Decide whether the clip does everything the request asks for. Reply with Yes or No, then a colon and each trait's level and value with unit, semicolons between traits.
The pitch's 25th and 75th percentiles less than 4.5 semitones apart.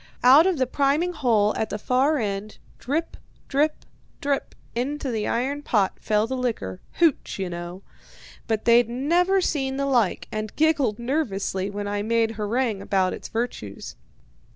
No: average, 5.2 semitones